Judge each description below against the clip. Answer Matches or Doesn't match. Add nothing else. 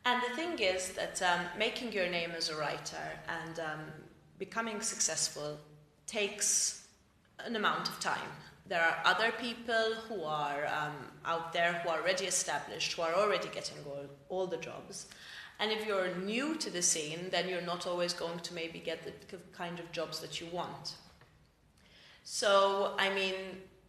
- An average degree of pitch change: Matches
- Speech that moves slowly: Doesn't match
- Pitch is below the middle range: Doesn't match